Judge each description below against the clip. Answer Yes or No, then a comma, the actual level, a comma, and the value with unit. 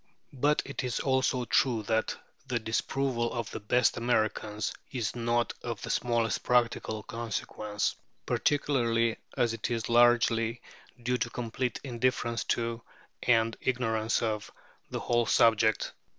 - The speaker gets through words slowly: Yes, slow, 130 wpm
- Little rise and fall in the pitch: Yes, narrow, 1.6 semitones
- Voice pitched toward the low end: Yes, low, 115 Hz